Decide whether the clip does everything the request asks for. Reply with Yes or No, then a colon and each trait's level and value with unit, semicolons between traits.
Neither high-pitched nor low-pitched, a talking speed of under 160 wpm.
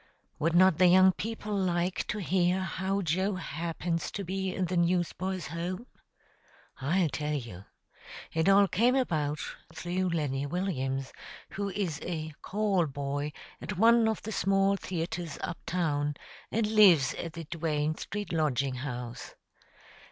Yes: medium, 175 Hz; average, 145 wpm